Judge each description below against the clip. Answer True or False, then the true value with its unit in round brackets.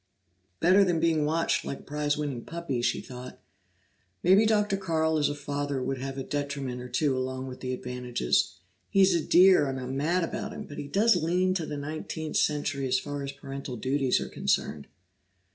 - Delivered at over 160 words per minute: True (195 wpm)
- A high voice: False (145 Hz)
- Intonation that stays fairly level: False (4.2 semitones)